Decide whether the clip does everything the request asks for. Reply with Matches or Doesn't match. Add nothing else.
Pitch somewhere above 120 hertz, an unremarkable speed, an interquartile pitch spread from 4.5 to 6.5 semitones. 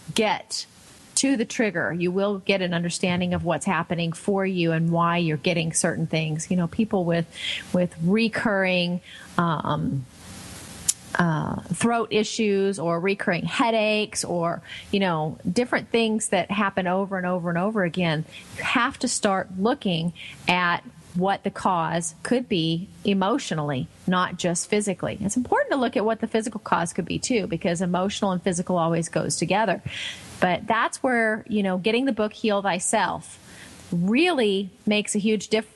Doesn't match